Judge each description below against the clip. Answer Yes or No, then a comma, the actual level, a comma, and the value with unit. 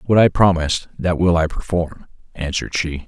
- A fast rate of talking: No, average, 175 wpm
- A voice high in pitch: No, very low, 85 Hz